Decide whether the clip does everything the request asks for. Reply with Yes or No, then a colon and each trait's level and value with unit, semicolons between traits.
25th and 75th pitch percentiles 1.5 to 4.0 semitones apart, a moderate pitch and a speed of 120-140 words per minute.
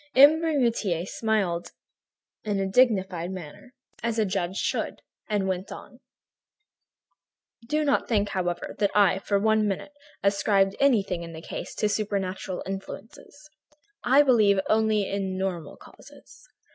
No: average, 2.8 semitones; high, 200 Hz; slow, 135 wpm